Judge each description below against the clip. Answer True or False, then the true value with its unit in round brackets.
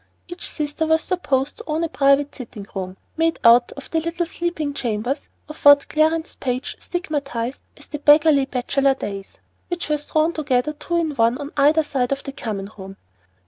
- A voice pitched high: True (285 Hz)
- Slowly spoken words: False (180 wpm)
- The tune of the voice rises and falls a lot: False (4.0 semitones)